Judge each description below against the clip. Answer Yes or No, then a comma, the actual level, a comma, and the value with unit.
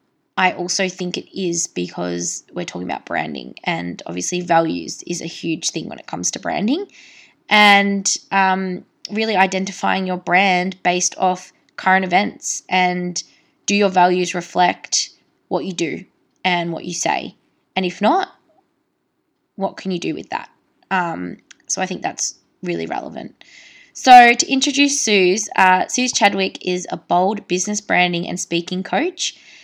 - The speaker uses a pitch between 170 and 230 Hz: Yes, medium, 185 Hz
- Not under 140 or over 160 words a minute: Yes, average, 150 wpm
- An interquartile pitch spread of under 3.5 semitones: Yes, average, 2.9 semitones